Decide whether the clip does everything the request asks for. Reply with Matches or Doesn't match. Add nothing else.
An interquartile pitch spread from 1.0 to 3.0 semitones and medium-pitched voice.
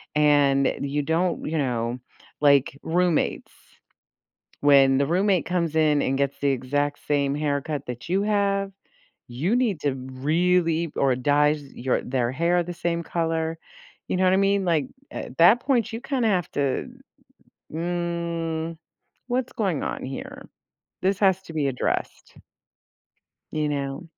Doesn't match